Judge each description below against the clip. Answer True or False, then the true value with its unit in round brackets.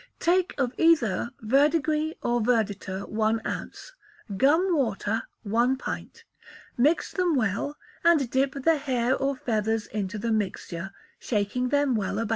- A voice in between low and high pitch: False (245 Hz)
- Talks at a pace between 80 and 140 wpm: True (135 wpm)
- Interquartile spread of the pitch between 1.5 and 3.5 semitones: False (5.2 semitones)